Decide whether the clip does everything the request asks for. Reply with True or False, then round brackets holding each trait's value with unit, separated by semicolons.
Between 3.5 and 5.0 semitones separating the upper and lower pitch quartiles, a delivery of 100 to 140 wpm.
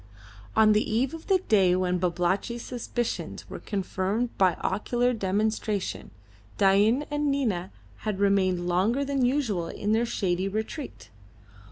True (4.3 semitones; 135 wpm)